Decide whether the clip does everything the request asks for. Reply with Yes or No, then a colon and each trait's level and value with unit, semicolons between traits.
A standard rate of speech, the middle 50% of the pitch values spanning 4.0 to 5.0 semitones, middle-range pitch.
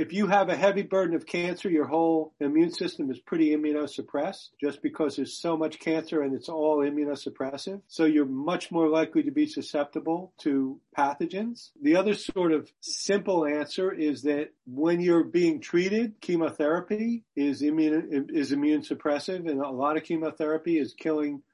Yes: average, 165 wpm; average, 4.4 semitones; medium, 160 Hz